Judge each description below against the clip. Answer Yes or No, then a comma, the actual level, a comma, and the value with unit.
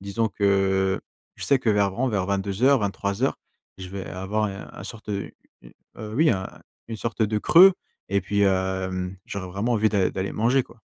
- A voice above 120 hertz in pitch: No, low, 100 Hz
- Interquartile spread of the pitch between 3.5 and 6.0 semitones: No, average, 2.8 semitones